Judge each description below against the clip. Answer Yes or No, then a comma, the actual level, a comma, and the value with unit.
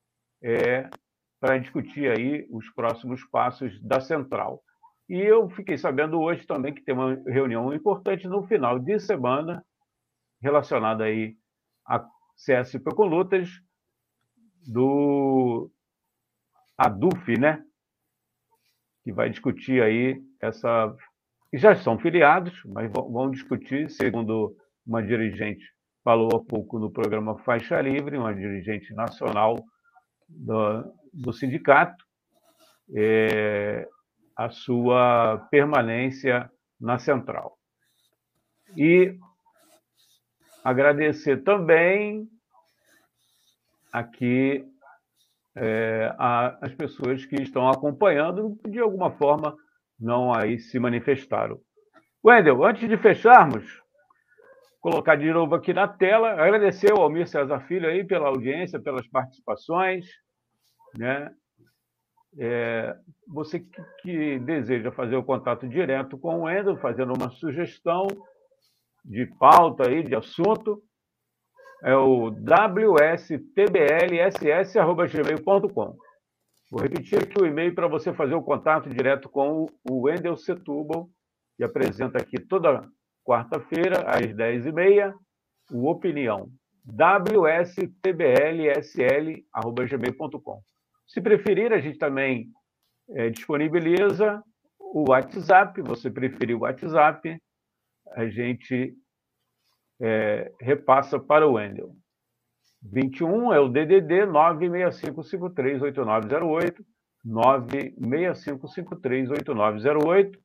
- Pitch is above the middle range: No, medium, 145 Hz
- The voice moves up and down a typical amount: No, wide, 6.8 semitones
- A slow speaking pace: Yes, slow, 95 wpm